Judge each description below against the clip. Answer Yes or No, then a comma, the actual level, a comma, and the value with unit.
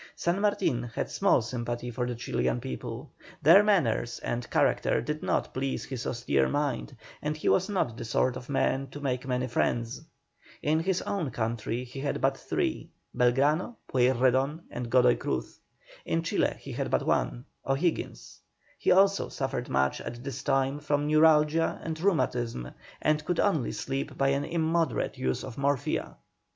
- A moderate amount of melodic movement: Yes, average, 4.1 semitones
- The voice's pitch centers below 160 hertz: Yes, low, 135 Hz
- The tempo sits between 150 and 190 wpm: Yes, average, 165 wpm